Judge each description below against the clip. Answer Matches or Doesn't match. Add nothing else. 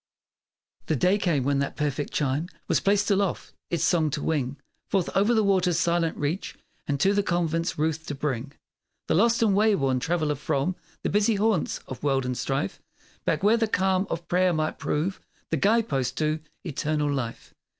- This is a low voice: Doesn't match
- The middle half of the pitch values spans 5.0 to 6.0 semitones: Matches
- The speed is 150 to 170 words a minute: Doesn't match